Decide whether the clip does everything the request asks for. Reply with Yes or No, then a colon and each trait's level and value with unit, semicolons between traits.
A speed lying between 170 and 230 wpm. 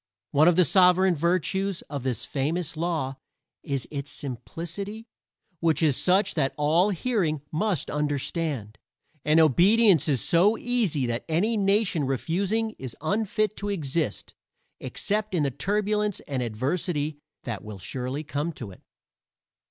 No: slow, 135 wpm